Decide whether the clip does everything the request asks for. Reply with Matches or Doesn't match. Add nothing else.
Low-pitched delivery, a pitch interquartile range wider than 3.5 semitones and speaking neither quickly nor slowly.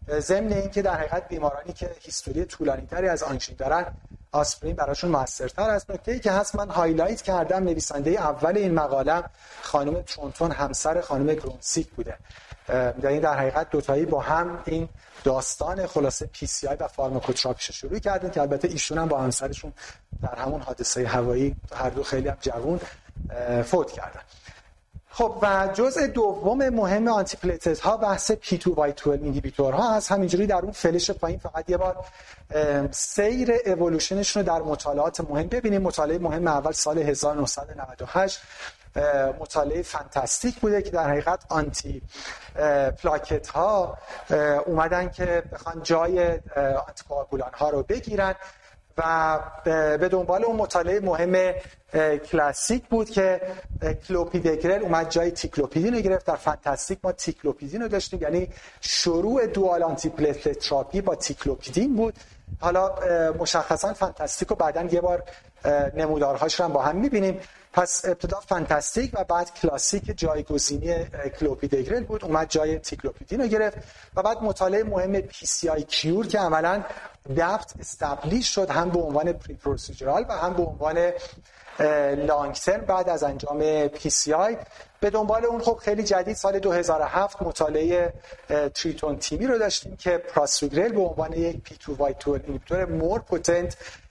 Doesn't match